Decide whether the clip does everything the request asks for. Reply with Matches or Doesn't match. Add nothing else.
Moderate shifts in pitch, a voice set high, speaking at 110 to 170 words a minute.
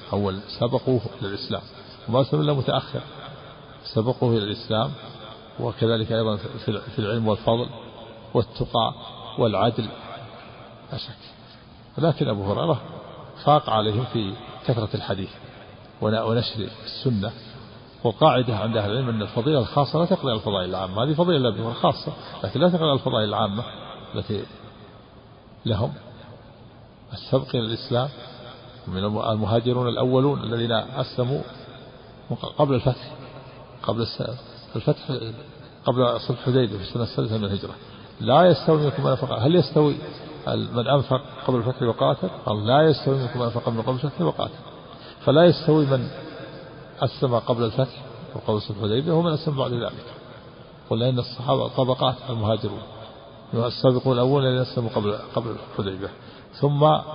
Doesn't match